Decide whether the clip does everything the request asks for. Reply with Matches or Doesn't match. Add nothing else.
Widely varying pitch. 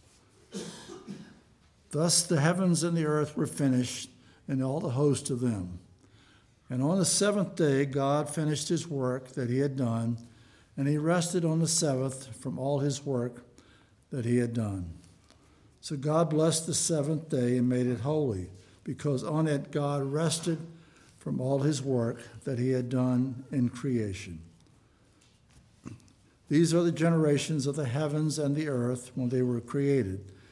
Doesn't match